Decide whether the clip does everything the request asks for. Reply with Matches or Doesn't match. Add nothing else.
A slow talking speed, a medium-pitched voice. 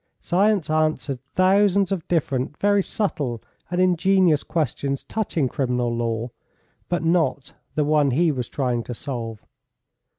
Matches